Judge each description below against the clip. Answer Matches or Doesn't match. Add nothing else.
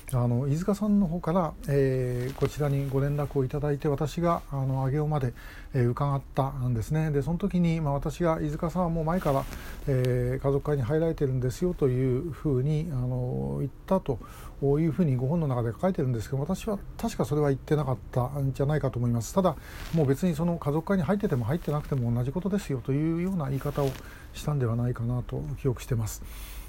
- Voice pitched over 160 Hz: Doesn't match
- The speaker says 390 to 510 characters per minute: Matches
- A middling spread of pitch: Matches